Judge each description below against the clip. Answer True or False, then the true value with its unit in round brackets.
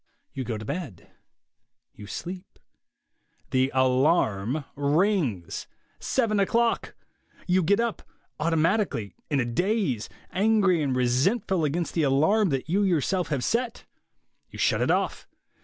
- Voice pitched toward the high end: False (160 Hz)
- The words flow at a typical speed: False (125 wpm)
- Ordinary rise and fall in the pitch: False (7.1 semitones)